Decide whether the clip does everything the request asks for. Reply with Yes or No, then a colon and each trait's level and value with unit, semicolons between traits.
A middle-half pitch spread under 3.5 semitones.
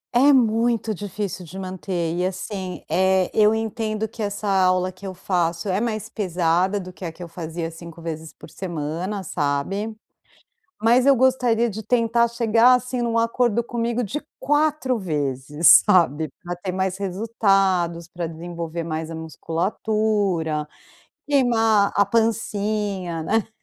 No: average, 4.7 semitones